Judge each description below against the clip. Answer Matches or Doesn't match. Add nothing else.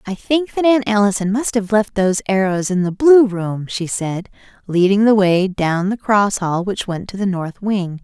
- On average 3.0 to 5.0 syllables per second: Matches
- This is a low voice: Doesn't match